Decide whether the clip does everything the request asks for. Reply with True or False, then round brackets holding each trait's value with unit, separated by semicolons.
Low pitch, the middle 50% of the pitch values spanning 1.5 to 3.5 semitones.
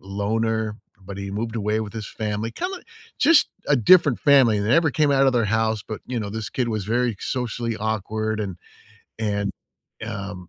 True (110 Hz; 2.8 semitones)